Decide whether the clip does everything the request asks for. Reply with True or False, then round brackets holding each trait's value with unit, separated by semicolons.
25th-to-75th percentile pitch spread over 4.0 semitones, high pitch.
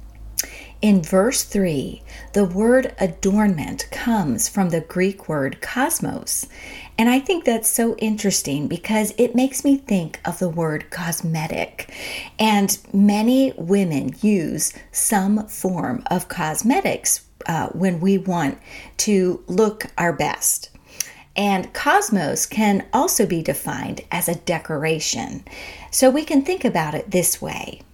True (4.6 semitones; 195 Hz)